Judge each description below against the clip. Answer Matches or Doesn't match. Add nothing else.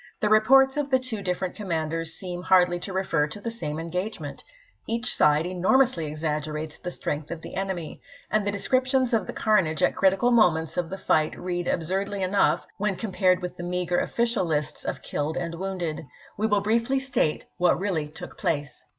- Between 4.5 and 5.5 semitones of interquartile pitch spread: Matches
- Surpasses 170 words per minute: Matches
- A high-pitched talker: Doesn't match